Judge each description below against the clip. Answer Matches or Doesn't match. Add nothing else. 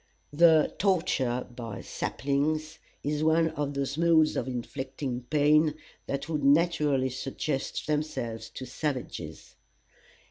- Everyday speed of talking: Doesn't match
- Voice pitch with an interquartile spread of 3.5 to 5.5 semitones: Doesn't match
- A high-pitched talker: Doesn't match